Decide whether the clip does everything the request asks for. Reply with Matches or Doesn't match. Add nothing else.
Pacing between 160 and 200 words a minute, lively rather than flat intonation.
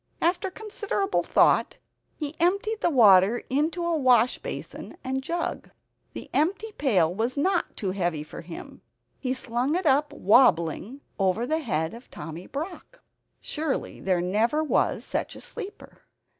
Doesn't match